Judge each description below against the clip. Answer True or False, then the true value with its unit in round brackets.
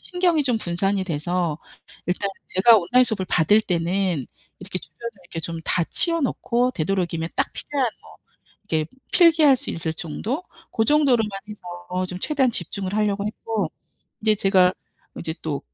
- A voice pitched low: False (195 Hz)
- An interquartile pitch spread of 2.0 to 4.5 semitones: False (5.4 semitones)